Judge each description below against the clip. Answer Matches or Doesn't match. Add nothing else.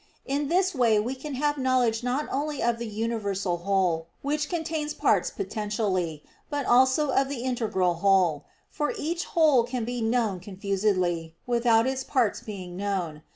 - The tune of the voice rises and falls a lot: Matches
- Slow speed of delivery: Doesn't match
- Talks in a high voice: Matches